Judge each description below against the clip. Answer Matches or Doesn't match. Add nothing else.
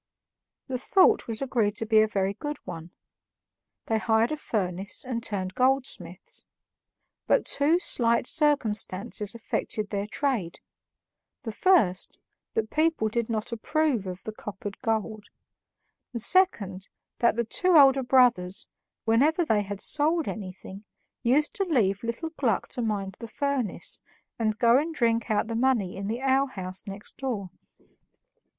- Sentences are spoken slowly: Doesn't match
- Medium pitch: Doesn't match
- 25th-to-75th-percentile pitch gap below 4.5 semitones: Doesn't match